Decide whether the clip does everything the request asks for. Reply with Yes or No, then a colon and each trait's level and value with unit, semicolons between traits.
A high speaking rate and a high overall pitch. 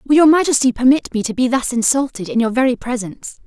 Yes: fast, 225 wpm; very high, 250 Hz